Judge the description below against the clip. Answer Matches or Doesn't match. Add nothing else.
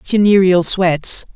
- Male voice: Doesn't match